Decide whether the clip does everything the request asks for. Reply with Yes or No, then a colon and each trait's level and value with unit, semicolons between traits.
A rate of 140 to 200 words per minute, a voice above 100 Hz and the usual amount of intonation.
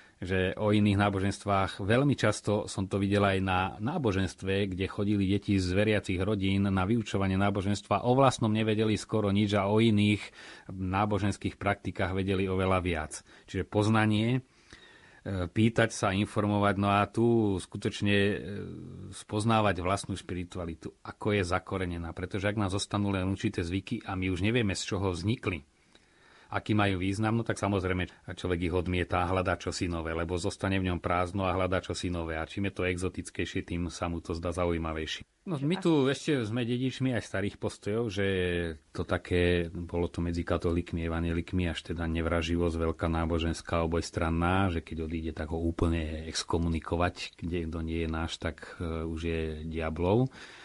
No: average, 160 wpm; very low, 95 Hz; average, 3.1 semitones